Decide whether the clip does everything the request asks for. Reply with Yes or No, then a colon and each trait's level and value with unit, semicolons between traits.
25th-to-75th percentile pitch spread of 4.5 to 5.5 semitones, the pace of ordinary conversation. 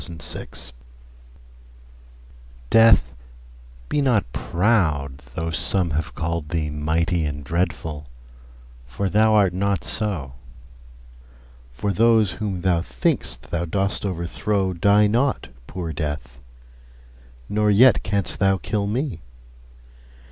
No: average, 4.9 semitones; slow, 105 wpm